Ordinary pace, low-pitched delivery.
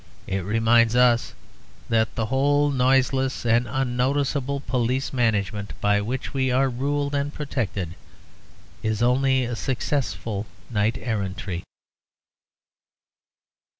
No: slow, 105 wpm; low, 125 Hz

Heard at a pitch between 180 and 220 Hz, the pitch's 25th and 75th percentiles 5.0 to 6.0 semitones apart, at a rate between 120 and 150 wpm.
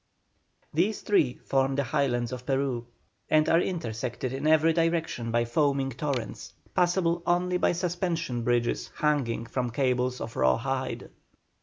No: low, 135 Hz; average, 5.3 semitones; average, 140 wpm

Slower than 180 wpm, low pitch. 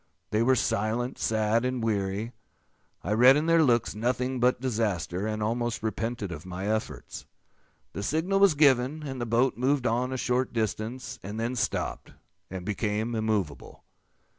Yes: average, 160 wpm; low, 115 Hz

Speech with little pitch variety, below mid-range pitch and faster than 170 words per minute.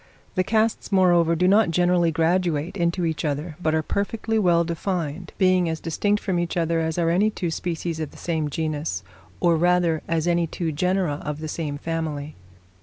No: narrow, 2.3 semitones; medium, 170 Hz; average, 185 wpm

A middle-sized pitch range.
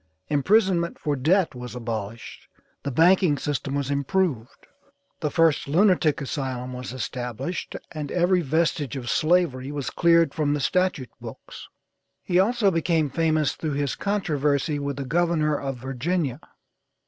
Yes: average, 4.1 semitones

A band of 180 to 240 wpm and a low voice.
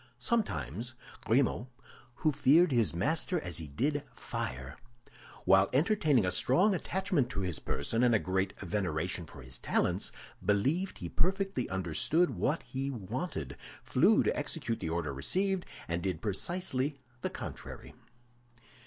No: slow, 135 wpm; low, 120 Hz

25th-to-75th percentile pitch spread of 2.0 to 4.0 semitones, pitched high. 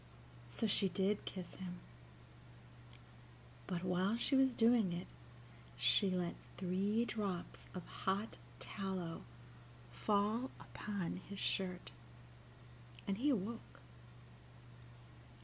Yes: average, 3.1 semitones; high, 195 Hz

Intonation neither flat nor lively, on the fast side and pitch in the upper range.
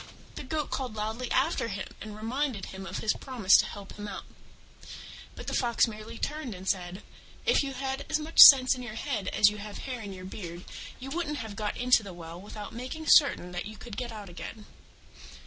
Yes: average, 4.4 semitones; fast, 215 wpm; high, 220 Hz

